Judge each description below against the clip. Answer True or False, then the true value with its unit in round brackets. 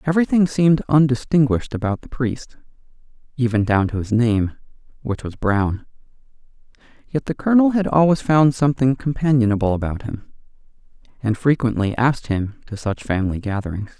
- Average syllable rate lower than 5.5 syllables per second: False (5.7 syllables/s)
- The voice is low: True (125 Hz)